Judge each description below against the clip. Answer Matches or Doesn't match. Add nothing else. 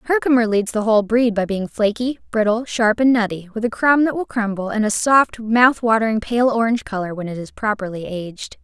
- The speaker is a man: Doesn't match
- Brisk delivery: Matches